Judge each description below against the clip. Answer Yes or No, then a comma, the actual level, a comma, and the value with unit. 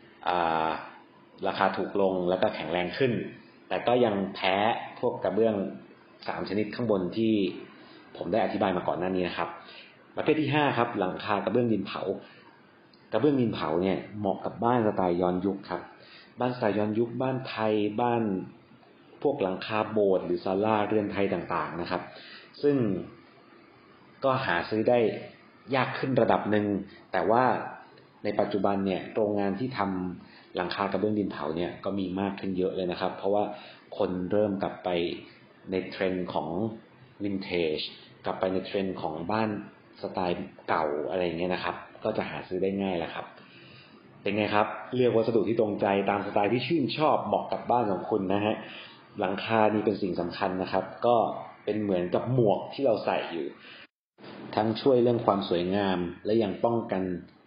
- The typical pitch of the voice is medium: No, low, 100 Hz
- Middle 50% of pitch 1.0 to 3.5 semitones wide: Yes, average, 2.9 semitones